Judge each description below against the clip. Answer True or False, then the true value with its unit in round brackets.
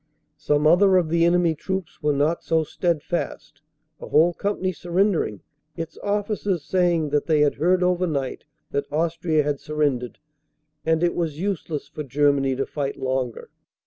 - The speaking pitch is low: False (160 Hz)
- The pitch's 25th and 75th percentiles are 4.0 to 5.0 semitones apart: False (3.3 semitones)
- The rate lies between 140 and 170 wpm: True (160 wpm)